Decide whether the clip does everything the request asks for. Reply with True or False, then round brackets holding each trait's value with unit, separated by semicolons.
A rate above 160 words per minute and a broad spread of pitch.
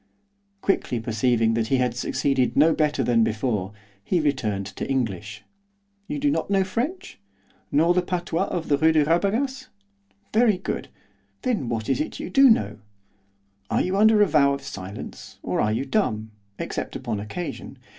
True (170 wpm; 8.7 semitones)